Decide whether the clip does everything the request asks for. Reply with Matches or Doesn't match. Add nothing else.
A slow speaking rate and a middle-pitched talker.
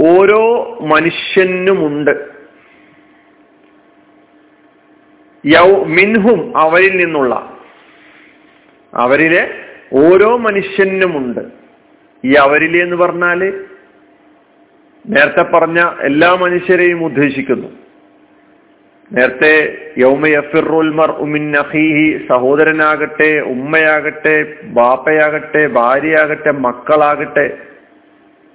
Matches